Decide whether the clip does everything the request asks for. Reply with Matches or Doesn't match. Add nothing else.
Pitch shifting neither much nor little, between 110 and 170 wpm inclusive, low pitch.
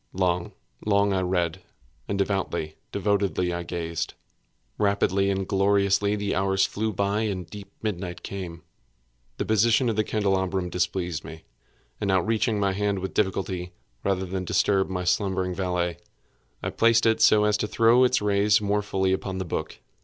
Doesn't match